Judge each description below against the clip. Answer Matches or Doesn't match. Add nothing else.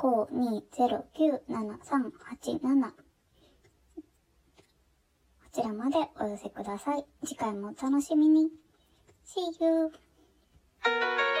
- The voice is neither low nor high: Doesn't match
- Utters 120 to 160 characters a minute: Matches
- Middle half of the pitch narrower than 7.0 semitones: Matches